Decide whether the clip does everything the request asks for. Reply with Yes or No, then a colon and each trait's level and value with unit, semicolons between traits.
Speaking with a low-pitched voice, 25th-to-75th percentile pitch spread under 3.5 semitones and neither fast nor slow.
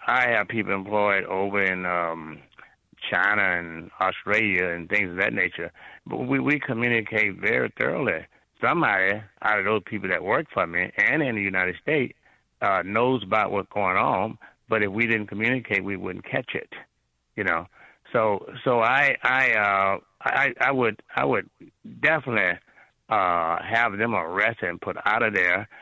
Yes: low, 100 Hz; average, 2.7 semitones; average, 165 wpm